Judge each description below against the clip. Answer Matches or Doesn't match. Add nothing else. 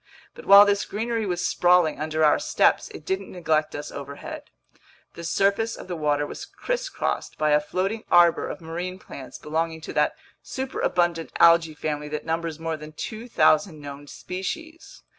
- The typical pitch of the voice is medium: Matches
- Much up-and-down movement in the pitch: Doesn't match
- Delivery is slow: Doesn't match